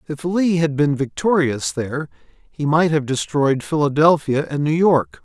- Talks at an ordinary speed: Yes, average, 160 wpm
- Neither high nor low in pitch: Yes, medium, 150 Hz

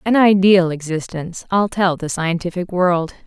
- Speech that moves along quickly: No, average, 145 wpm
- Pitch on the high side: No, medium, 180 Hz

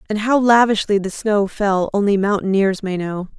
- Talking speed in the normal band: Yes, average, 175 wpm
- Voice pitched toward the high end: Yes, high, 205 Hz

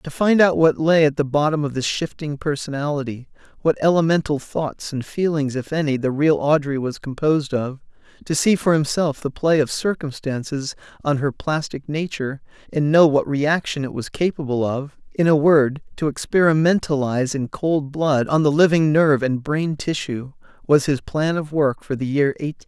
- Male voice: Yes, male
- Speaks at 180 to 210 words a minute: Yes, average, 185 wpm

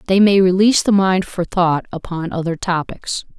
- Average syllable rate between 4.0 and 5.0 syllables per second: Yes, 4.9 syllables/s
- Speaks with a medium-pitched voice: Yes, medium, 180 Hz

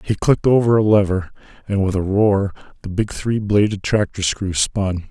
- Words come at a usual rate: Yes, average, 190 wpm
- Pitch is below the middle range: Yes, low, 100 Hz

